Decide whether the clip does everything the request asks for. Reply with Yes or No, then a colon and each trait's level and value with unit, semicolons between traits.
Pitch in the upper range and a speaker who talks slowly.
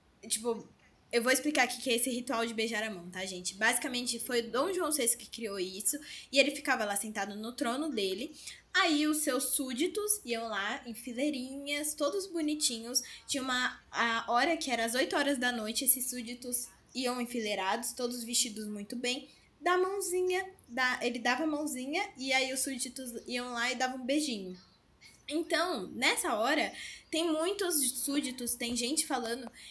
No: very high, 255 Hz; average, 175 wpm